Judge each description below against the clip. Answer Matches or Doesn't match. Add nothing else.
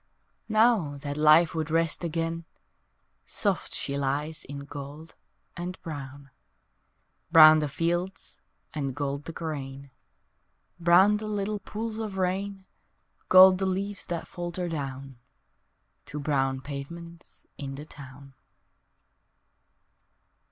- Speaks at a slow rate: Matches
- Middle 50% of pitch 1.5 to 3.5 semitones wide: Doesn't match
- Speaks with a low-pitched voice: Doesn't match